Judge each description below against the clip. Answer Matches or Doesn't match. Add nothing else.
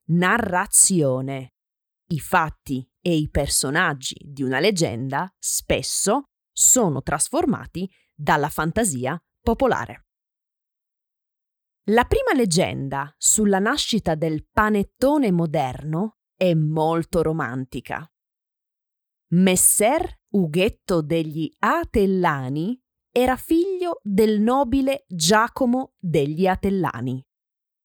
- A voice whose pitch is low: Doesn't match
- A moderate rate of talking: Doesn't match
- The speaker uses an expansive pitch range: Matches